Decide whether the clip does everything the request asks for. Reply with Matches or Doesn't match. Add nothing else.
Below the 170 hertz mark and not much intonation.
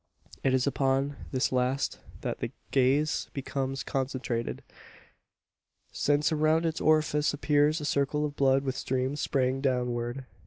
Matches